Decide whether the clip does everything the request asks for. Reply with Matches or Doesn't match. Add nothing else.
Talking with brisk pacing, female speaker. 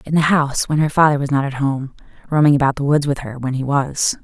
Matches